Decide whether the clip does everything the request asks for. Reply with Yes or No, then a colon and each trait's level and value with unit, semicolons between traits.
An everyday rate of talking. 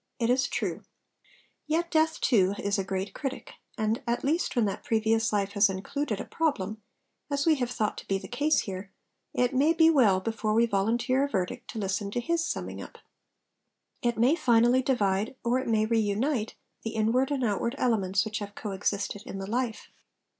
Yes: average, 190 wpm